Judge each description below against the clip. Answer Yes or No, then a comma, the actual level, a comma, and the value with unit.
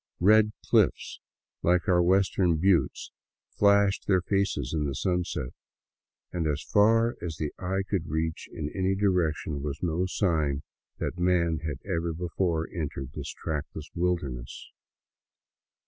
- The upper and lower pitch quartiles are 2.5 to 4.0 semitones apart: Yes, average, 3.4 semitones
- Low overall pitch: Yes, very low, 85 Hz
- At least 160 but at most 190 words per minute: No, slow, 135 wpm